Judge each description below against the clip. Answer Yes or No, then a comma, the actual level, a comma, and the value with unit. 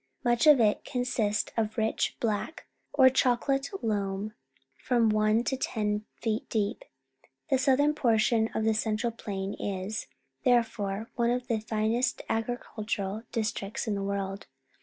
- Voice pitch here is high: Yes, high, 220 Hz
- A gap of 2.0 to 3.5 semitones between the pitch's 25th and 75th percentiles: Yes, narrow, 2.6 semitones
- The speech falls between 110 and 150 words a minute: Yes, average, 140 wpm